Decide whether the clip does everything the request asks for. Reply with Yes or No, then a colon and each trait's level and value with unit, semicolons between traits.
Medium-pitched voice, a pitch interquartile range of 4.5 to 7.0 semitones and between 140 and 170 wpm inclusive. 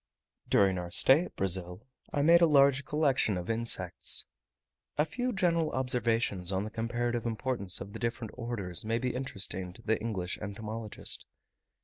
No: low, 115 Hz; average, 5.0 semitones; average, 155 wpm